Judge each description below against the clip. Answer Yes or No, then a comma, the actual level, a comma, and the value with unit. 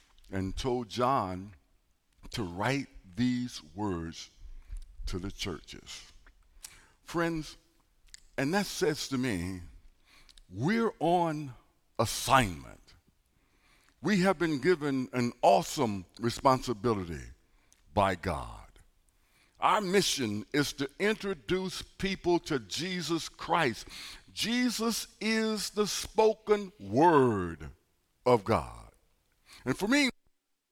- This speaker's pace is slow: Yes, slow, 90 wpm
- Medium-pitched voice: No, low, 125 Hz